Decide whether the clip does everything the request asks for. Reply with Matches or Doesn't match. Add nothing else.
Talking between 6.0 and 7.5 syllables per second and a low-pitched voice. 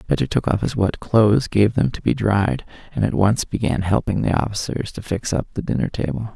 Doesn't match